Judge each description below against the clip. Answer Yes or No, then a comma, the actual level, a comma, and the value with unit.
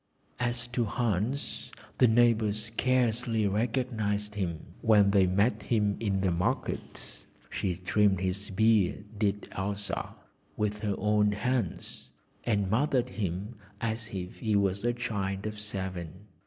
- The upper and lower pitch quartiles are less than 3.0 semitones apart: Yes, narrow, 2.6 semitones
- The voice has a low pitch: Yes, low, 105 Hz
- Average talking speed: No, slow, 130 wpm